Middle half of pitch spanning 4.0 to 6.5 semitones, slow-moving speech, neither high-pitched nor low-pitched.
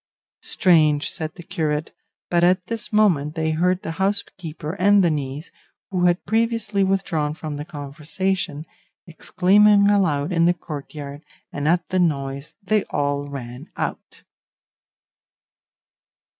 Yes: average, 4.4 semitones; slow, 130 wpm; medium, 165 Hz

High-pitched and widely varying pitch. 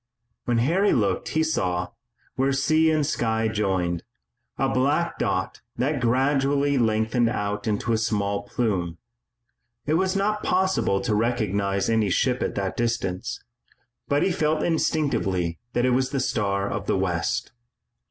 No: low, 120 Hz; wide, 5.9 semitones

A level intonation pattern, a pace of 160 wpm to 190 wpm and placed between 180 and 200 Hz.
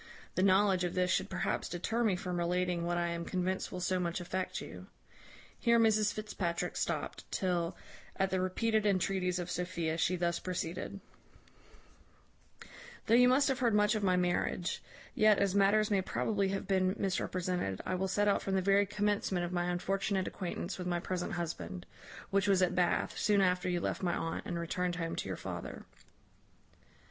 Yes: narrow, 2.2 semitones; average, 180 wpm; medium, 185 Hz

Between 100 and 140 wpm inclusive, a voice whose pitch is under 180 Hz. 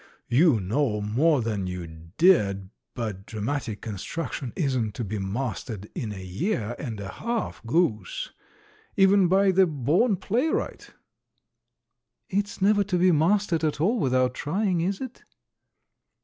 Yes: slow, 135 wpm; medium, 140 Hz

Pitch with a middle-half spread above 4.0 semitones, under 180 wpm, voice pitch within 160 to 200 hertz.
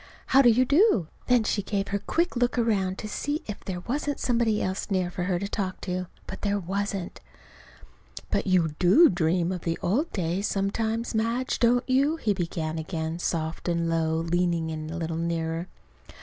No: wide, 5.4 semitones; average, 185 wpm; high, 190 Hz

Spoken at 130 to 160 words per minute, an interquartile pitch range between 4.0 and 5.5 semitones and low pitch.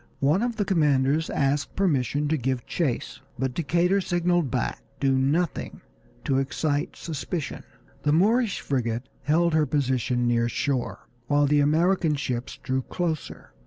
No: average, 140 wpm; average, 4.3 semitones; medium, 145 Hz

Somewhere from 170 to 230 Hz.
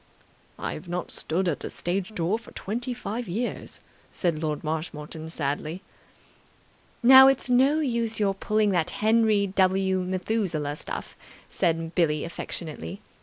Yes: medium, 185 Hz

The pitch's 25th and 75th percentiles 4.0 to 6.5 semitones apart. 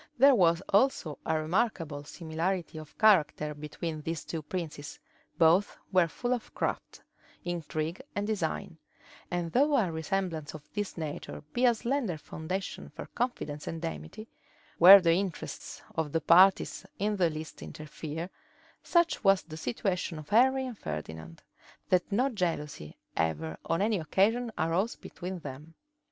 Yes: average, 4.6 semitones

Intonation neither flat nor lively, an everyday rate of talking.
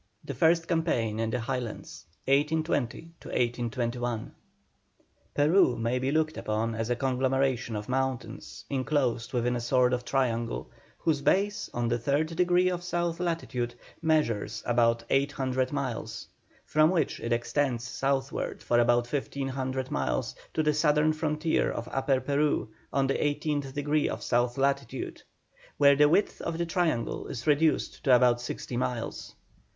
Yes: average, 4.0 semitones; average, 150 wpm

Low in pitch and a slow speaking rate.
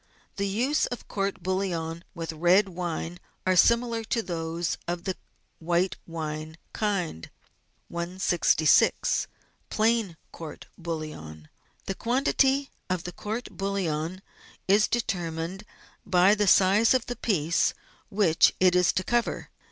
No: medium, 185 Hz; slow, 120 wpm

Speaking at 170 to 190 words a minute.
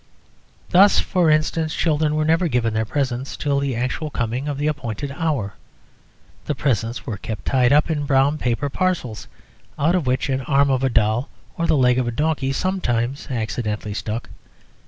Yes: average, 175 wpm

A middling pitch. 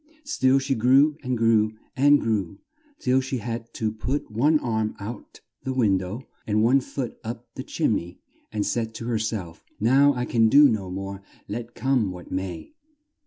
No: low, 115 Hz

